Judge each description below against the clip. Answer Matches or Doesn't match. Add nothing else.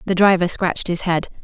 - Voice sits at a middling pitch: Matches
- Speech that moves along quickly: Matches